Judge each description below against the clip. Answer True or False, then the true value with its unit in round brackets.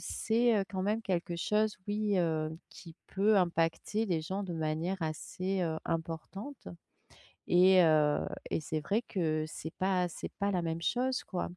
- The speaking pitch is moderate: True (180 Hz)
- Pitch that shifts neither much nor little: True (3.8 semitones)